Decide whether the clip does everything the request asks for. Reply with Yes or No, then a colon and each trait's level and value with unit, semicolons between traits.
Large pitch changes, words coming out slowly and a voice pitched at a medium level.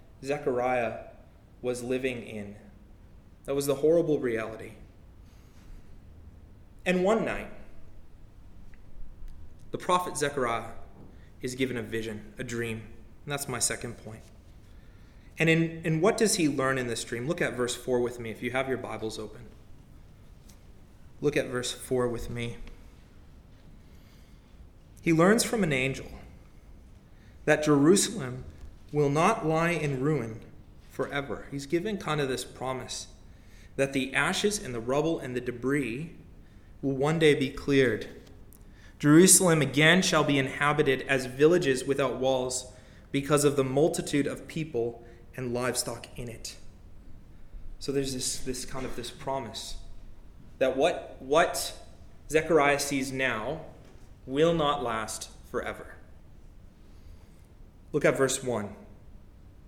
No: wide, 6.2 semitones; slow, 130 wpm; low, 125 Hz